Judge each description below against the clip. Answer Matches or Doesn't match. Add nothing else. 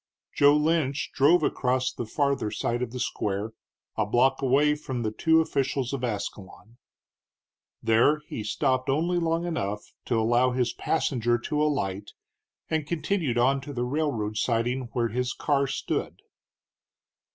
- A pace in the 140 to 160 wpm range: Matches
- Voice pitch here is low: Matches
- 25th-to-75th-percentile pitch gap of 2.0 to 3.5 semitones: Doesn't match